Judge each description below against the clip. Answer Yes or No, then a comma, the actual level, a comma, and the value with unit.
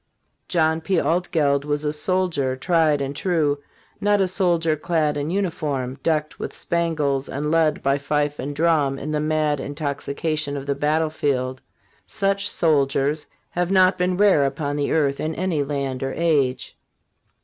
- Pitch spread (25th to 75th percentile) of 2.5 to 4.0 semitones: Yes, average, 3.0 semitones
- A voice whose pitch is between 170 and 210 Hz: No, medium, 150 Hz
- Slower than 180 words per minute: Yes, average, 155 wpm